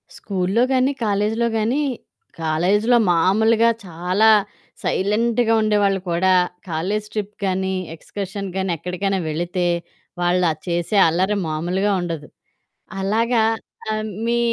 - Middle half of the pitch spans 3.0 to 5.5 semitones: Yes, average, 3.5 semitones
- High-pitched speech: Yes, high, 195 Hz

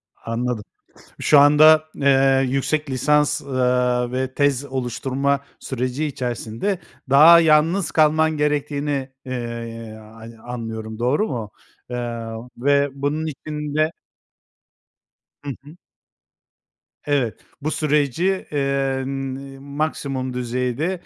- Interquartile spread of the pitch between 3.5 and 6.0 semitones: No, average, 3.1 semitones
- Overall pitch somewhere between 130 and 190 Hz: Yes, low, 135 Hz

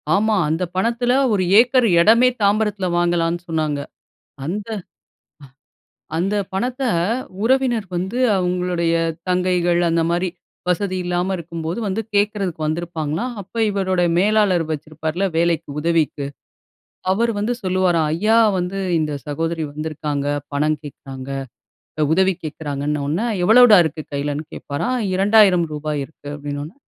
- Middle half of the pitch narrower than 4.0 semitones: No, average, 4.4 semitones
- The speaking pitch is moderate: Yes, medium, 175 Hz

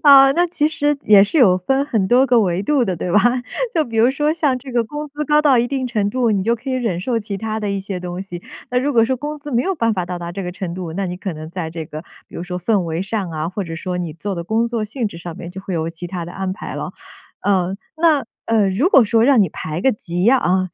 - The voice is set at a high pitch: Yes, high, 210 Hz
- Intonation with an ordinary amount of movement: No, wide, 6.2 semitones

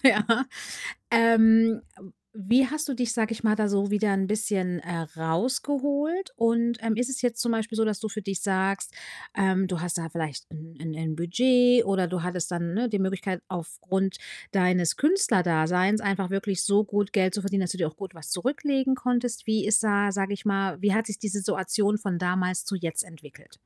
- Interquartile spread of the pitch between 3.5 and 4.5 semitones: Yes, average, 3.9 semitones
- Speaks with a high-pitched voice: Yes, high, 200 Hz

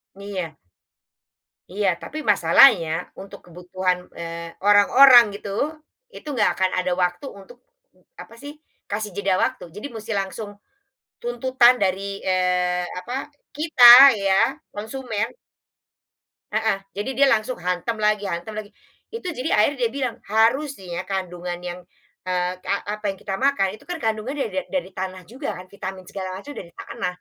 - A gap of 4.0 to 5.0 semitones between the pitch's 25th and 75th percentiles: Yes, average, 4.6 semitones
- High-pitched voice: Yes, high, 205 Hz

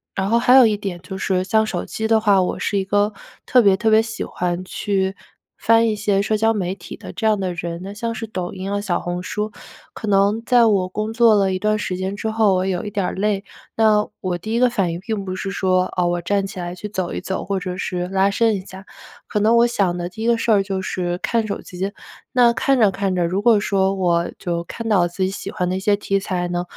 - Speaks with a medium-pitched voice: No, high, 195 Hz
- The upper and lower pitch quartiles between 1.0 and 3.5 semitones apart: Yes, average, 2.8 semitones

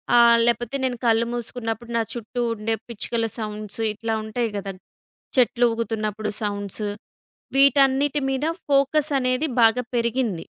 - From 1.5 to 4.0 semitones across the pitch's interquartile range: Yes, narrow, 2.6 semitones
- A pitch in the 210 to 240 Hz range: Yes, high, 235 Hz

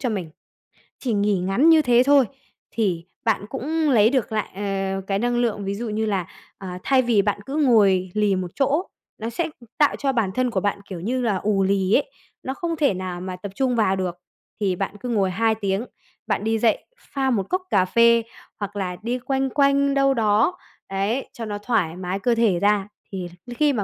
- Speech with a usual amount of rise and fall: Yes, average, 4.7 semitones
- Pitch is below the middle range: No, high, 215 Hz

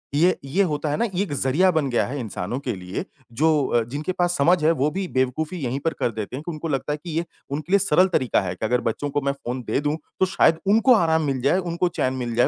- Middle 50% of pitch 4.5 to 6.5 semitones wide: Yes, average, 5.1 semitones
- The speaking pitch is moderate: Yes, medium, 145 Hz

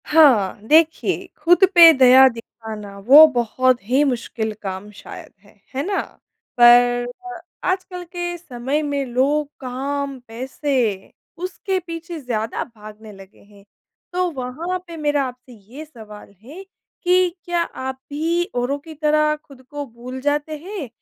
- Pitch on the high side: Yes, very high, 275 Hz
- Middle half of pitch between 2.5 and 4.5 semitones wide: No, average, 5.0 semitones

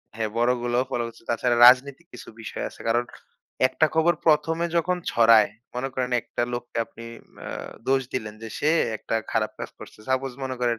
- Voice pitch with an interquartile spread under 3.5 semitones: Yes, narrow, 2.6 semitones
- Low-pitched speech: Yes, low, 125 Hz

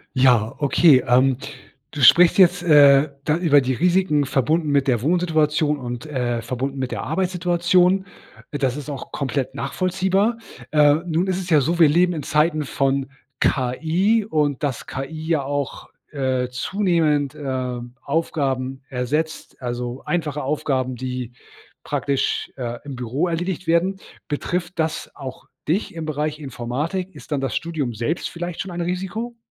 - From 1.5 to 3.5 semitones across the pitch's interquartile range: No, average, 4.5 semitones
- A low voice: No, medium, 150 Hz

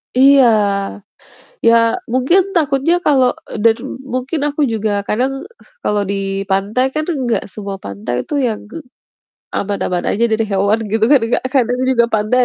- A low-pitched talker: No, high, 230 Hz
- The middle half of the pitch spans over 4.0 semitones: Yes, average, 4.8 semitones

